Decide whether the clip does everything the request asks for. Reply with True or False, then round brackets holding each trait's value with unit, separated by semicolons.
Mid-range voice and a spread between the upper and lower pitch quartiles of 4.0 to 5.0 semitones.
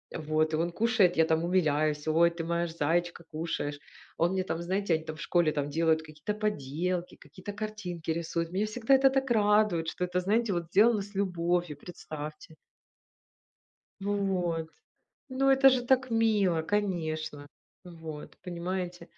True (175 Hz; 4.3 semitones)